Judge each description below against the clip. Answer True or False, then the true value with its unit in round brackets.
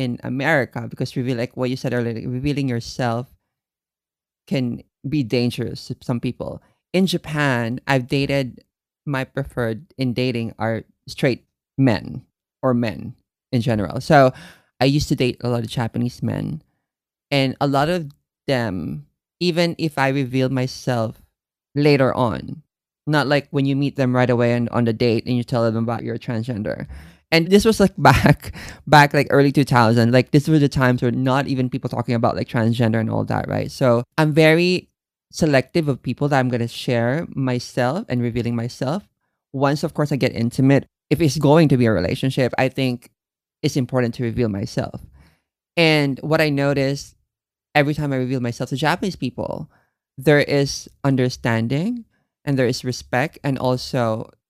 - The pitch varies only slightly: False (3.1 semitones)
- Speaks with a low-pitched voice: True (130 Hz)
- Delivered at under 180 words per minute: True (170 wpm)